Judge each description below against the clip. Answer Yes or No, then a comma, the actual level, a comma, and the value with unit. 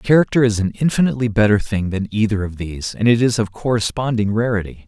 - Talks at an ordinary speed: Yes, average, 195 wpm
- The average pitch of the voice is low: Yes, low, 110 Hz